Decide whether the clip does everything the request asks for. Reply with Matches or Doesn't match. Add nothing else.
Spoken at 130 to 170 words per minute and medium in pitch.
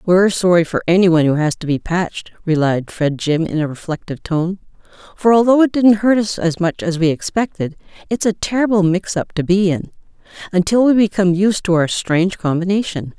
Doesn't match